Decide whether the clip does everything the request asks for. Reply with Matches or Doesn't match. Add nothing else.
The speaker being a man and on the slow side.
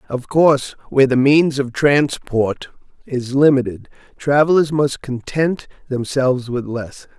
Matches